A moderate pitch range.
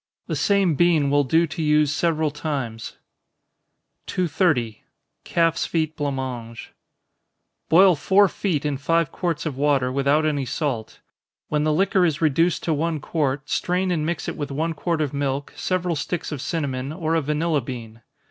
Yes: average, 3.2 semitones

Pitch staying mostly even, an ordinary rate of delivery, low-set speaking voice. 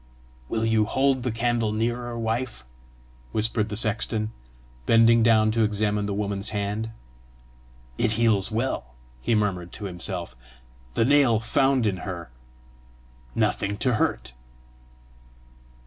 No: narrow, 2.3 semitones; slow, 120 wpm; low, 110 Hz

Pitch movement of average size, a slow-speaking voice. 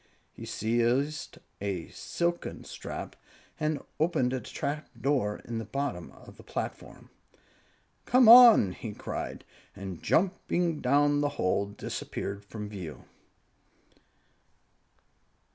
No: wide, 6.9 semitones; slow, 110 wpm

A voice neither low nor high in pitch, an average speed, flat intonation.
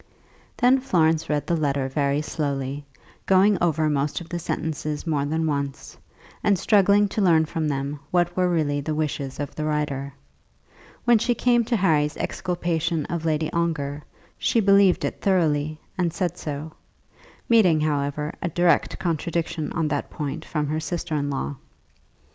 No: medium, 155 Hz; average, 160 wpm; average, 3.2 semitones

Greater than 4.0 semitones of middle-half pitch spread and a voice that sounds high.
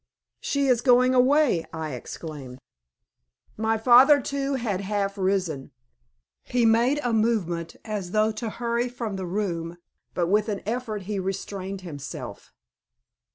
Yes: average, 4.7 semitones; high, 215 Hz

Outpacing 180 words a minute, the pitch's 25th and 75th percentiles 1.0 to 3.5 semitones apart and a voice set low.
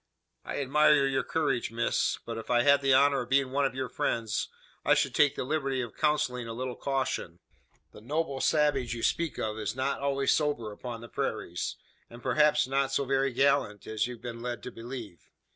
Yes: average, 200 wpm; average, 3.0 semitones; low, 130 Hz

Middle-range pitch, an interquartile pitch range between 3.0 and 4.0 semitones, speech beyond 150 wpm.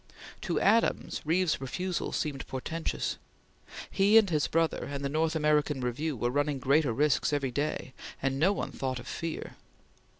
Yes: medium, 150 Hz; average, 3.3 semitones; average, 160 wpm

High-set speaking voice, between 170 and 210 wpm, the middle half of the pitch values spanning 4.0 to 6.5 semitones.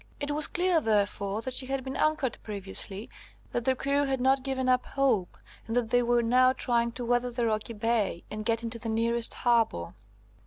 No: high, 240 Hz; average, 200 wpm; average, 2.7 semitones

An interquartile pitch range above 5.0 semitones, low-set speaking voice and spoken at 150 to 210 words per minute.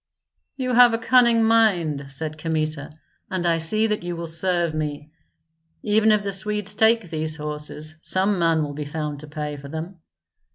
No: wide, 5.5 semitones; medium, 165 Hz; average, 175 wpm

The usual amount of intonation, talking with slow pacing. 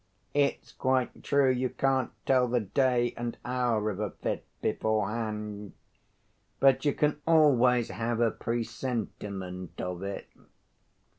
Yes: average, 3.5 semitones; slow, 125 wpm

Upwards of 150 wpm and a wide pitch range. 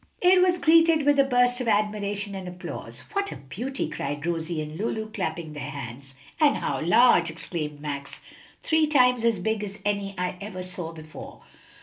Yes: average, 180 wpm; wide, 7.7 semitones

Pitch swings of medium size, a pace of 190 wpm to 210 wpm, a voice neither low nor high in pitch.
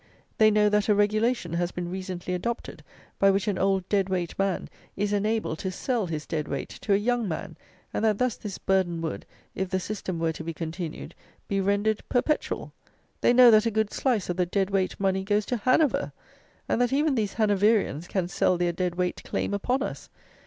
No: average, 3.2 semitones; fast, 205 wpm; high, 195 Hz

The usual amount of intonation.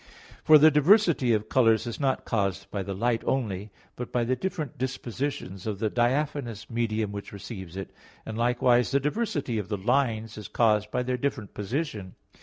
Yes: average, 4.1 semitones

